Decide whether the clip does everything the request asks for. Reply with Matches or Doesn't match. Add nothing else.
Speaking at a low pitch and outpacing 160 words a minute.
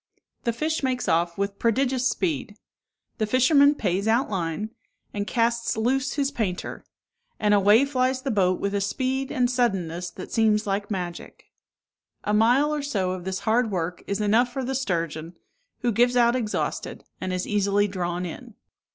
Doesn't match